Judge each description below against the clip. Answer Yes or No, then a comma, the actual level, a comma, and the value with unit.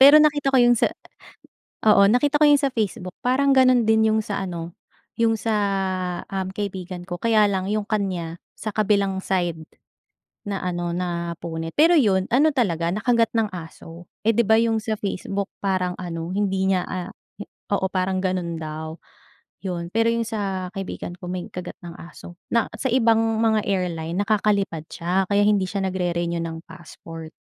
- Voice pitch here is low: No, high, 195 Hz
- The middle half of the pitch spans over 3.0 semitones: Yes, average, 4.0 semitones